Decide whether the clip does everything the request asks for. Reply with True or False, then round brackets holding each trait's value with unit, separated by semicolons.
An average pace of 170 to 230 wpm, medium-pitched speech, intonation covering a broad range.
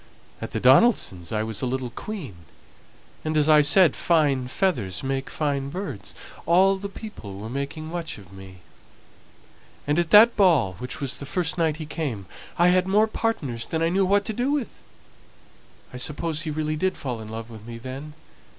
True (190 wpm; 150 Hz; 6.6 semitones)